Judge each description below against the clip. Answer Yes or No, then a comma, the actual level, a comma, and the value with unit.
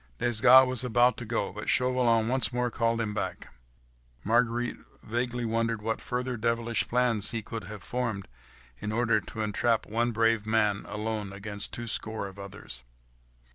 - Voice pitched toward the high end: No, low, 115 Hz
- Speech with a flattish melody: Yes, narrow, 2.2 semitones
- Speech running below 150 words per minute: No, average, 160 wpm